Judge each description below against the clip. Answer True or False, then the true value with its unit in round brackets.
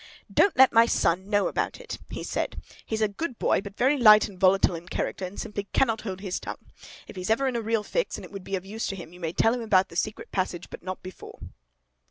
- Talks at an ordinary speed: False (260 wpm)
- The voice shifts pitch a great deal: False (3.4 semitones)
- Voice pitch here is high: True (205 Hz)